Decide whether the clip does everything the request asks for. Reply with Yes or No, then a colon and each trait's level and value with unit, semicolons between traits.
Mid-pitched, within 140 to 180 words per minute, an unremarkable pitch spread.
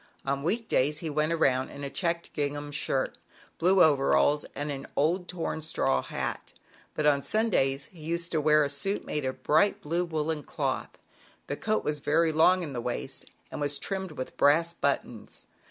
No: medium, 150 Hz; average, 190 wpm; average, 3.1 semitones